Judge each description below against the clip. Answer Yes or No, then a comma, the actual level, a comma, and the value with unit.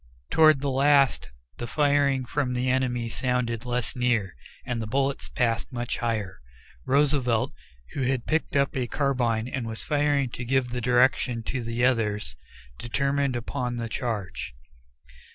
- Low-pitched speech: Yes, low, 125 Hz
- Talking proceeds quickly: No, average, 150 wpm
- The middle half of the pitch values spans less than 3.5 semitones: Yes, average, 2.8 semitones